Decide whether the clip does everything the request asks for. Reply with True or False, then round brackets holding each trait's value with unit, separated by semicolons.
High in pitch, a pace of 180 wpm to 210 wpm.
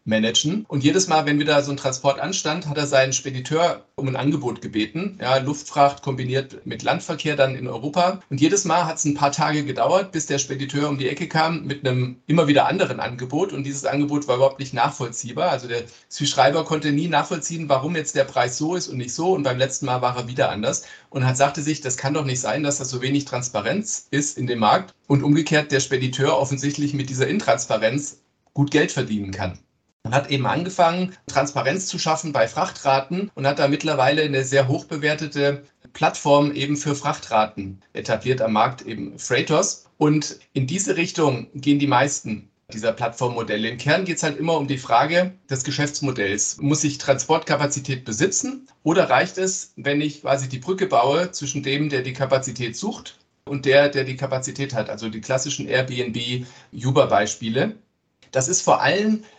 False (140 Hz; 190 wpm)